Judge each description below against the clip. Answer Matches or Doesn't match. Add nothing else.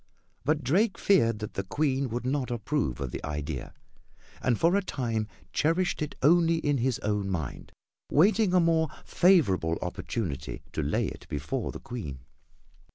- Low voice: Matches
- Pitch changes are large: Matches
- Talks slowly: Doesn't match